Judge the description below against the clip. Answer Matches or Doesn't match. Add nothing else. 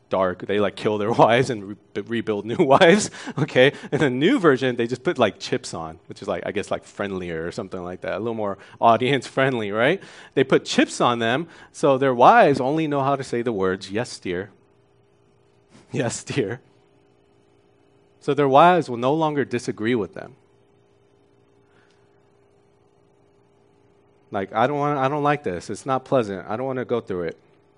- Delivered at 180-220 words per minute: Matches